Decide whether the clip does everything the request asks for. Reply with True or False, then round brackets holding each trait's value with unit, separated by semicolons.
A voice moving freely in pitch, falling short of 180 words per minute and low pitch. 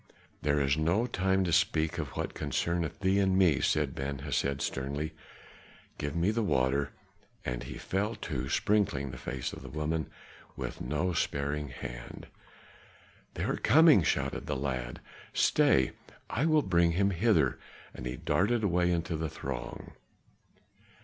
True (5.7 semitones; 150 wpm; 80 Hz)